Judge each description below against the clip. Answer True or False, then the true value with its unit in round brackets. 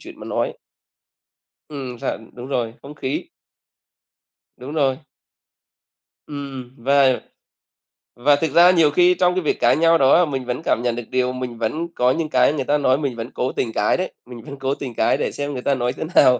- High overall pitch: False (135 Hz)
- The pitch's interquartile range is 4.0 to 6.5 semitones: False (3.0 semitones)